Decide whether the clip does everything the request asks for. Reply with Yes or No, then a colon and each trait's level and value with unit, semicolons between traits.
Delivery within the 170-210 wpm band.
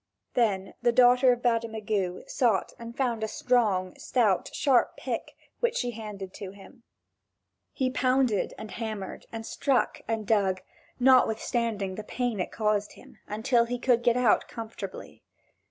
No: average, 145 wpm